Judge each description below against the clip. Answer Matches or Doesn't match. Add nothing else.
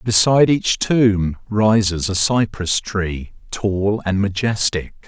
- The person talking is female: Doesn't match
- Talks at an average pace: Doesn't match